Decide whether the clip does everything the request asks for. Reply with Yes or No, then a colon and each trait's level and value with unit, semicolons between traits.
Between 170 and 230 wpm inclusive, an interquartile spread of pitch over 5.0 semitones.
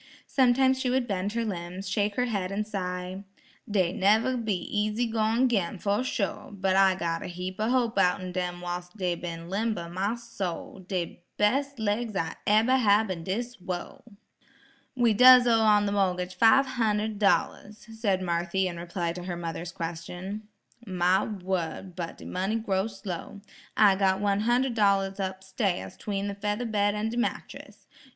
No: average, 175 wpm; average, 3.4 semitones